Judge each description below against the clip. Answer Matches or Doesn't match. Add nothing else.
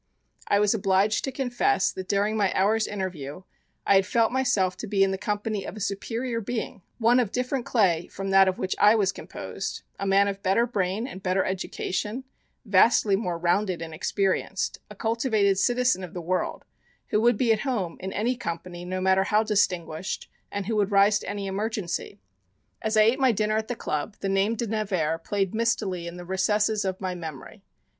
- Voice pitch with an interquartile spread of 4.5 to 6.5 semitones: Doesn't match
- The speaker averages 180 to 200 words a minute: Matches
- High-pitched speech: Matches